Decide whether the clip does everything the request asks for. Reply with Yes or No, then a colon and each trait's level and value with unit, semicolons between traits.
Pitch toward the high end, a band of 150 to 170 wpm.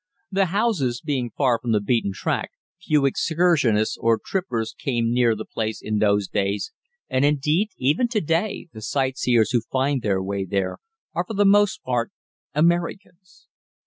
No: low, 130 Hz; average, 160 wpm